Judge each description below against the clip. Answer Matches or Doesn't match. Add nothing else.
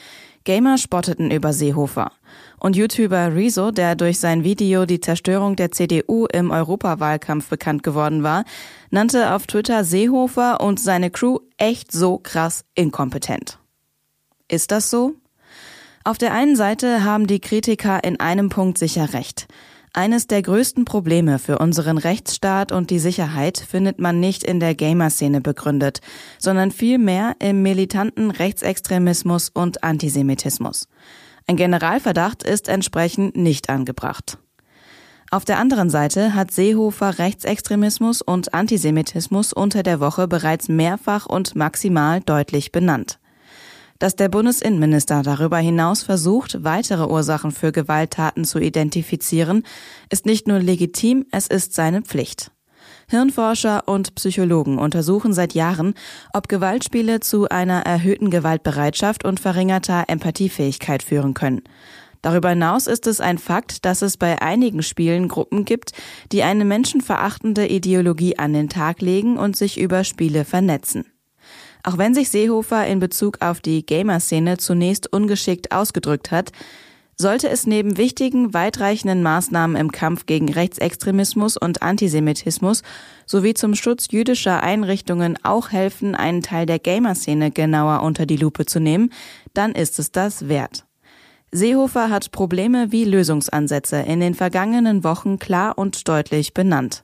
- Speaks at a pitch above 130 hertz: Matches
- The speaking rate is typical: Matches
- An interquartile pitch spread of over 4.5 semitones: Doesn't match